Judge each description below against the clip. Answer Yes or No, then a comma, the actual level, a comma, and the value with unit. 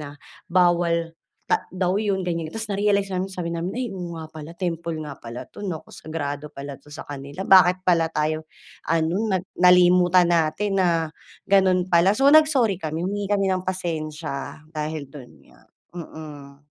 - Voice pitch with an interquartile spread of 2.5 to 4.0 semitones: Yes, average, 3.2 semitones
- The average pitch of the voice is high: No, medium, 170 Hz